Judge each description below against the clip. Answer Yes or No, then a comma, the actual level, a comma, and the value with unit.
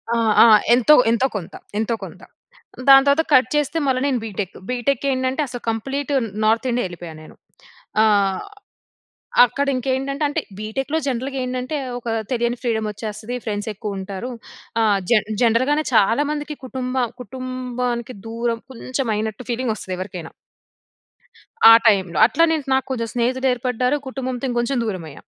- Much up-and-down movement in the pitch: No, average, 3.2 semitones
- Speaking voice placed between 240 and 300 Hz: Yes, high, 245 Hz